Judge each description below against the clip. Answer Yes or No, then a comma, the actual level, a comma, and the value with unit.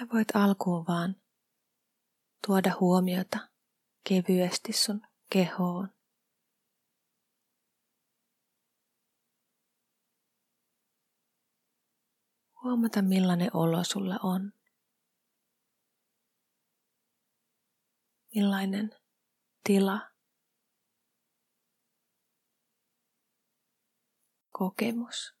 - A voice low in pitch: No, high, 195 Hz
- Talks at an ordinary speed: No, slow, 40 wpm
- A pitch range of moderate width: Yes, average, 3.3 semitones